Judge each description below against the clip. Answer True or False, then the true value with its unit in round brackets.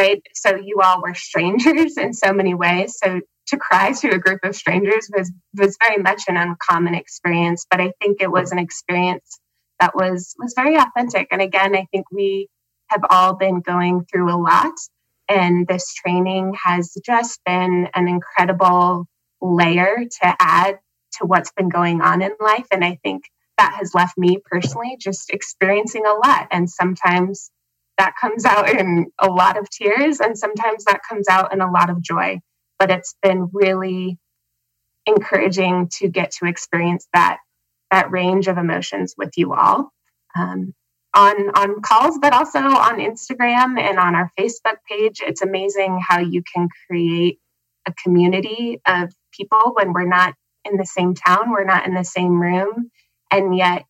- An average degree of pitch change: False (2.1 semitones)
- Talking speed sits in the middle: True (170 wpm)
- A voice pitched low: False (185 Hz)